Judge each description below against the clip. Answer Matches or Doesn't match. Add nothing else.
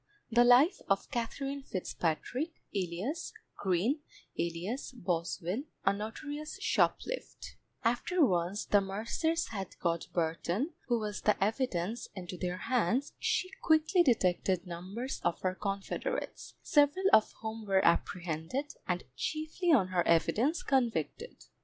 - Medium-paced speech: Doesn't match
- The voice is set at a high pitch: Matches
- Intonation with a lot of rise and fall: Matches